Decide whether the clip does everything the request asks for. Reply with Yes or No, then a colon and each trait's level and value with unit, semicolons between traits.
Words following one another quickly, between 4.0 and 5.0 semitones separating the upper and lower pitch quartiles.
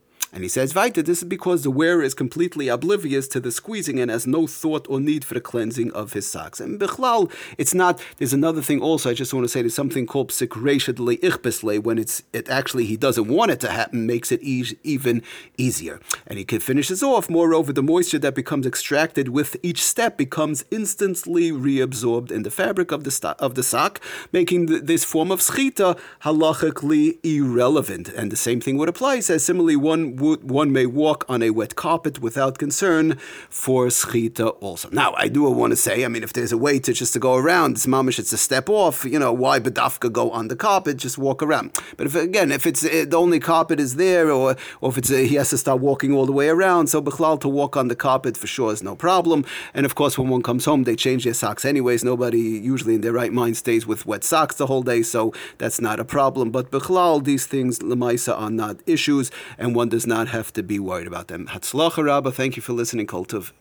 Yes: fast, 225 wpm; average, 4.7 semitones